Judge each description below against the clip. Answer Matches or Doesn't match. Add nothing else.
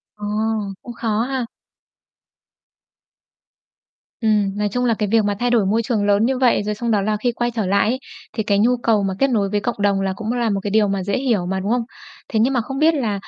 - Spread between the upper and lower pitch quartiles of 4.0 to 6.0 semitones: Doesn't match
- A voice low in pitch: Doesn't match